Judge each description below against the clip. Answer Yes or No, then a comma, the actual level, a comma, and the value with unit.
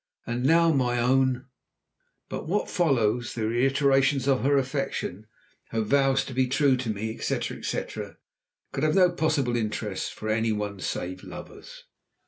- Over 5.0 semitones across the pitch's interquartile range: No, average, 3.7 semitones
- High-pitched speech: No, low, 130 Hz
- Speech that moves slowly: No, average, 155 wpm